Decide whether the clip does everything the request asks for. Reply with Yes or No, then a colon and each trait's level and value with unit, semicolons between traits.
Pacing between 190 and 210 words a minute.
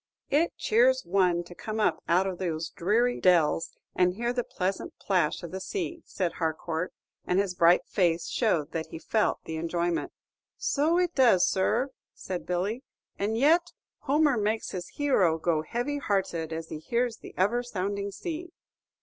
No: average, 165 wpm